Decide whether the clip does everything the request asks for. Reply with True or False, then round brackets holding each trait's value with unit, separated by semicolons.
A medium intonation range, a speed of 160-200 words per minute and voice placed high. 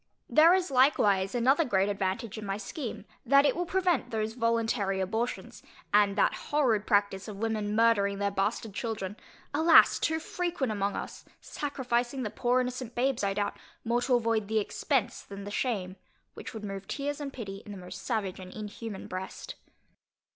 True (4.3 semitones; 175 wpm; 220 Hz)